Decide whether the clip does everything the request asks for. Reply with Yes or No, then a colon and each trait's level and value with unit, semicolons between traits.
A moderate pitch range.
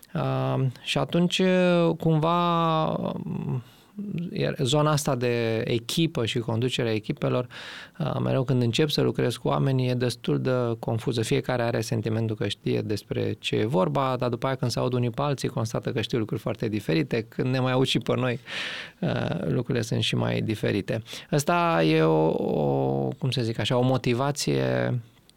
Yes: average, 4.3 semitones